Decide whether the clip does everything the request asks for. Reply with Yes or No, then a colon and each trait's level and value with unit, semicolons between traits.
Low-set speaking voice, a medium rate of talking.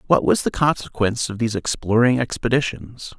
Yes: low, 115 Hz; average, 150 wpm